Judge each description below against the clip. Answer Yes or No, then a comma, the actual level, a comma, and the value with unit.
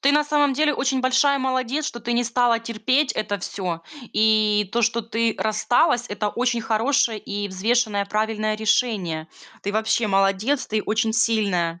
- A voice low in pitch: No, high, 225 Hz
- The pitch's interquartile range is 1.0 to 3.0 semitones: No, average, 3.4 semitones